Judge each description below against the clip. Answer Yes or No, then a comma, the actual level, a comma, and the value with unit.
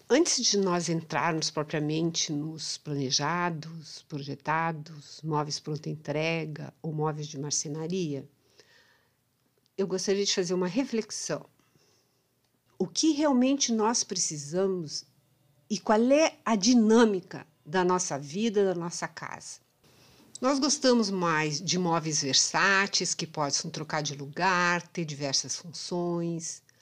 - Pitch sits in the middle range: Yes, medium, 165 Hz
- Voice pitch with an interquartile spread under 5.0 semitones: Yes, average, 4.3 semitones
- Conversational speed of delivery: No, slow, 115 wpm